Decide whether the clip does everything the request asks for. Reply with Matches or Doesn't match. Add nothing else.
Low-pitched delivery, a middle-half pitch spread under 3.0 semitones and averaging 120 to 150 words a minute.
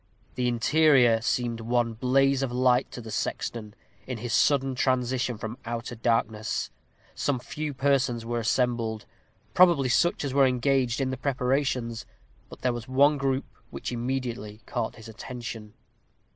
Matches